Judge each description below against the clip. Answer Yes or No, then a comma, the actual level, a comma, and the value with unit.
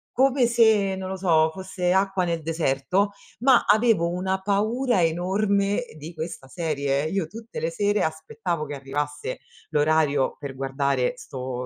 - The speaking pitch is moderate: Yes, medium, 175 Hz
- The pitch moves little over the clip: No, average, 5.3 semitones